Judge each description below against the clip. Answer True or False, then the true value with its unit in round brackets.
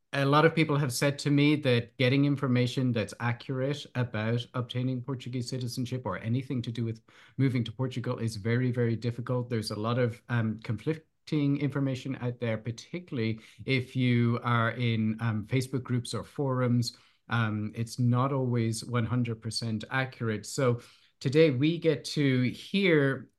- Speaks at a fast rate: False (155 wpm)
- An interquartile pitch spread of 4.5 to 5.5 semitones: False (2.7 semitones)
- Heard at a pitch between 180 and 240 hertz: False (125 Hz)